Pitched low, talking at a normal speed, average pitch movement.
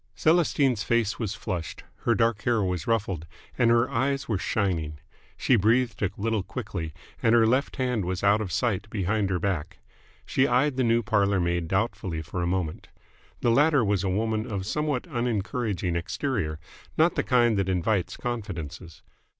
Yes: low, 110 Hz; average, 170 wpm; average, 4.5 semitones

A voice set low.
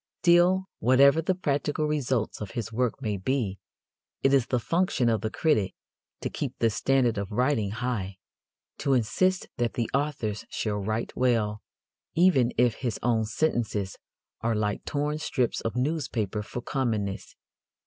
Yes: low, 120 Hz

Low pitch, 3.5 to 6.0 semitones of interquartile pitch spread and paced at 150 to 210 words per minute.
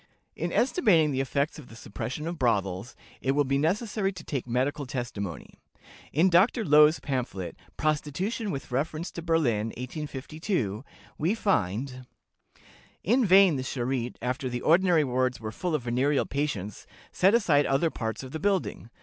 No: medium, 145 Hz; average, 5.2 semitones; average, 160 wpm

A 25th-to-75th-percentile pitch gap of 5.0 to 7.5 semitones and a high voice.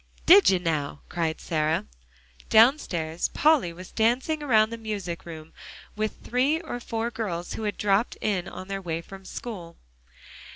Yes: wide, 5.5 semitones; high, 200 Hz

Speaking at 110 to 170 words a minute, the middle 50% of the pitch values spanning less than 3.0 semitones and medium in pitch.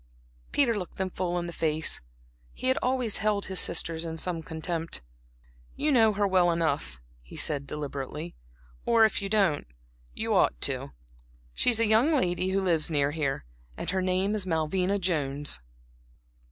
No: average, 165 wpm; average, 4.4 semitones; medium, 180 Hz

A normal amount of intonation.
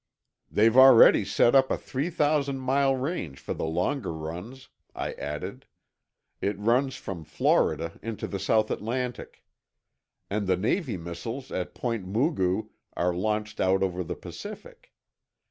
No: wide, 6.3 semitones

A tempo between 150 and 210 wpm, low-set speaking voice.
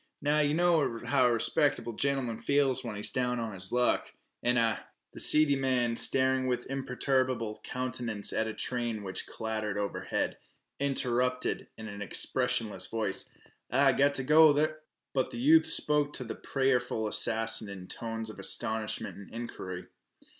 Yes: average, 160 wpm; low, 125 Hz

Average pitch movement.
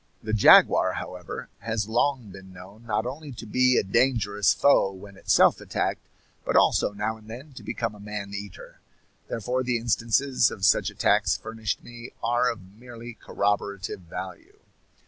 Yes: average, 3.1 semitones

